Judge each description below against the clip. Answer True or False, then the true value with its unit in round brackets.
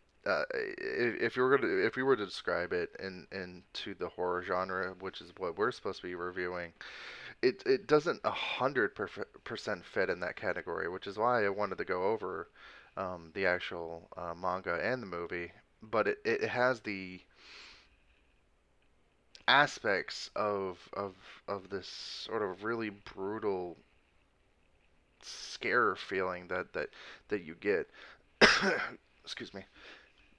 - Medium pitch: False (100 Hz)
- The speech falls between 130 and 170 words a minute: True (145 wpm)